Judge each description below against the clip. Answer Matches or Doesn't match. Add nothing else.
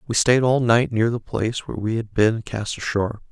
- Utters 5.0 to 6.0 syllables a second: Matches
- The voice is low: Matches